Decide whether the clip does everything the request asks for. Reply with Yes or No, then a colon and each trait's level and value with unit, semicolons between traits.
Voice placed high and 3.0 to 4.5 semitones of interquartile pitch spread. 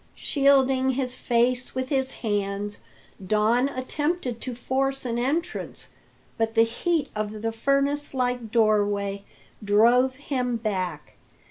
Yes: high, 245 Hz; average, 3.8 semitones